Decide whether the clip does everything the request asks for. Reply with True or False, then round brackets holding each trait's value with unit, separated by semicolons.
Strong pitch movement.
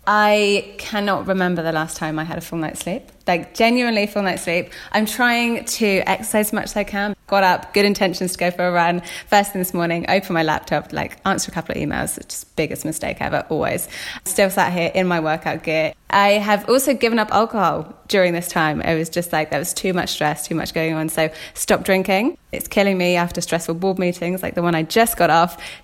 False (3.4 semitones)